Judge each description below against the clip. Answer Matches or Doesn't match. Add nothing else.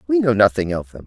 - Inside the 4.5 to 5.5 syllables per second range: Doesn't match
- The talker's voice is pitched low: Matches